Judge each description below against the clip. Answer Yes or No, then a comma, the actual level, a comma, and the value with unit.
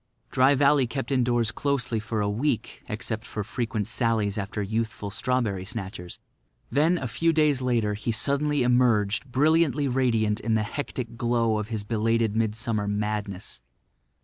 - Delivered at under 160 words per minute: Yes, average, 150 wpm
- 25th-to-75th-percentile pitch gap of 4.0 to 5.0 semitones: No, average, 3.5 semitones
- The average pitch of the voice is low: Yes, low, 115 Hz